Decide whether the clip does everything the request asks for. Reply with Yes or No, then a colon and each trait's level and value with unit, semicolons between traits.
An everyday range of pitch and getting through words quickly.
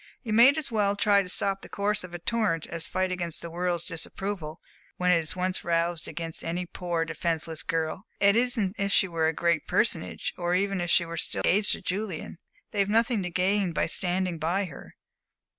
Yes: average, 3.2 semitones; fast, 215 wpm